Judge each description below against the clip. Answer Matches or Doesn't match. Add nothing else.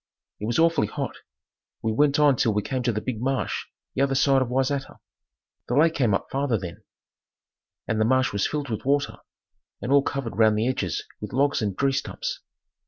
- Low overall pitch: Matches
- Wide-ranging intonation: Doesn't match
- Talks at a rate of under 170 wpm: Doesn't match